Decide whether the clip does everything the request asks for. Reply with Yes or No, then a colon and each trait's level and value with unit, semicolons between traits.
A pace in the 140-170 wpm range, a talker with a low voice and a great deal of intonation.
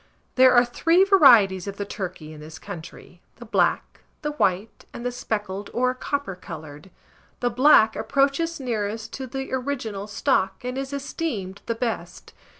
No: average, 155 wpm; high, 230 Hz; wide, 5.7 semitones